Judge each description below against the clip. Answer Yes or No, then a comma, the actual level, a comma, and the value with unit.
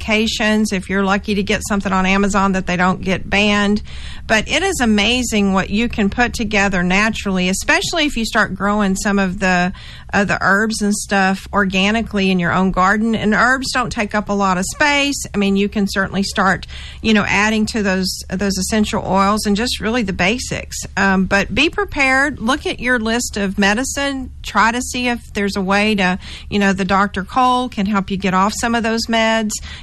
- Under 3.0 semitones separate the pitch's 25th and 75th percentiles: Yes, narrow, 2.6 semitones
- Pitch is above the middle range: Yes, high, 205 Hz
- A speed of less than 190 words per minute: No, fast, 205 wpm